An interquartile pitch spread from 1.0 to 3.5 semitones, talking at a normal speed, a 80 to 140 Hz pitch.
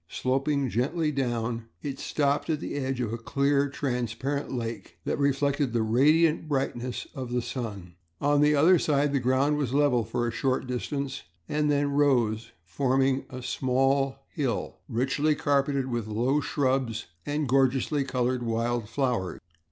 Yes: average, 2.9 semitones; average, 150 wpm; low, 135 Hz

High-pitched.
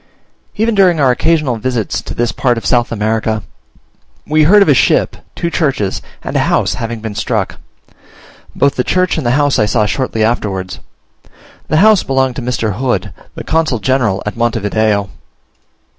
No: low, 125 Hz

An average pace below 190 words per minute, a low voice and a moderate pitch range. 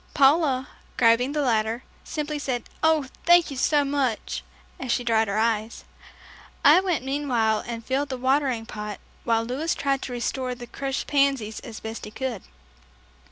No: average, 160 wpm; very high, 255 Hz; average, 3.7 semitones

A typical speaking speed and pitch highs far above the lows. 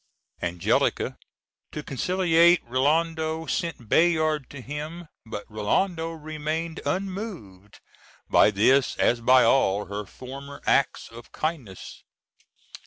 No: slow, 105 wpm; wide, 5.7 semitones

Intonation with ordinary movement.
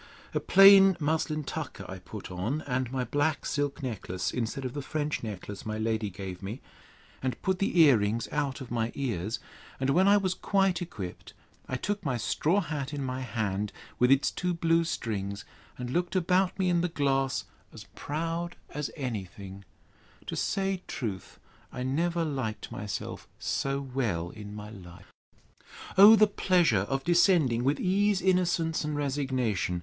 No: wide, 7.4 semitones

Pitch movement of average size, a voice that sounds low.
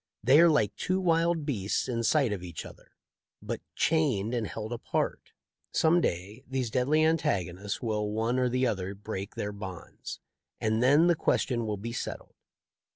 No: wide, 6.1 semitones; low, 115 Hz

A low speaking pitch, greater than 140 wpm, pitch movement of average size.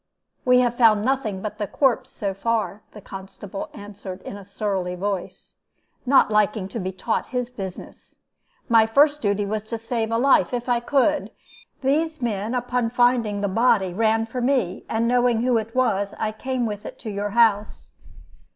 No: high, 225 Hz; average, 175 wpm; average, 3.4 semitones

